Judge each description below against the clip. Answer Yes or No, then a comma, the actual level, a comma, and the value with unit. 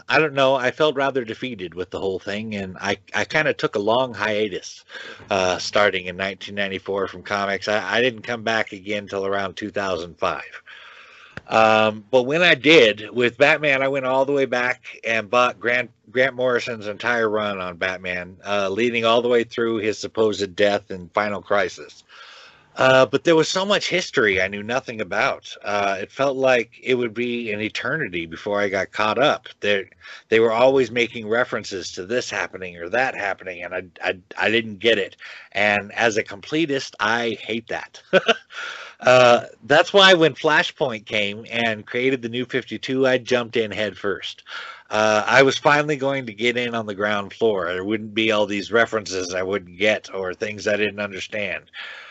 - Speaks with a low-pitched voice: Yes, low, 110 Hz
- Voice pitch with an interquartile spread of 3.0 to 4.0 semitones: Yes, average, 3.6 semitones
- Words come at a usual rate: Yes, average, 185 wpm